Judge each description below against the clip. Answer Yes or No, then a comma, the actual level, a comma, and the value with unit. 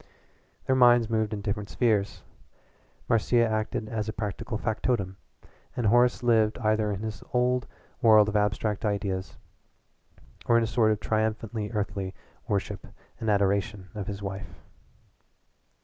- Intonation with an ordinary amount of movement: No, narrow, 2.0 semitones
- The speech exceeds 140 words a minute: No, slow, 135 wpm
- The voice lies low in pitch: Yes, low, 110 Hz